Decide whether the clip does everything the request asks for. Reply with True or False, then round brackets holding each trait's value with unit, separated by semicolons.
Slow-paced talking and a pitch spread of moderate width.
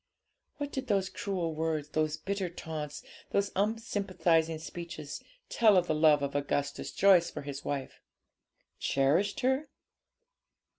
True (130 wpm; 4.9 semitones)